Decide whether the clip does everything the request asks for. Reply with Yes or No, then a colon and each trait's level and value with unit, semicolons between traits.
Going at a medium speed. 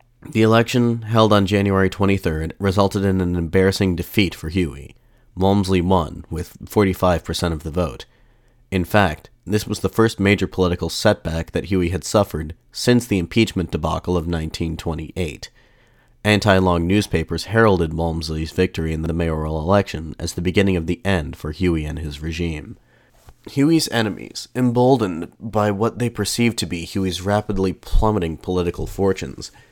Yes: average, 150 wpm